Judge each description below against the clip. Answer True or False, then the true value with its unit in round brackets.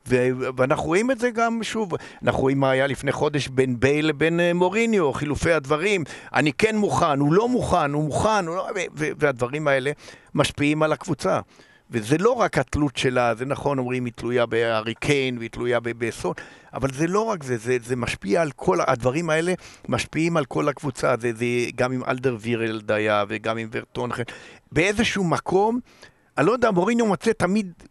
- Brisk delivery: True (170 wpm)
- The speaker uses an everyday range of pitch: False (5.7 semitones)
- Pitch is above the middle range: False (140 Hz)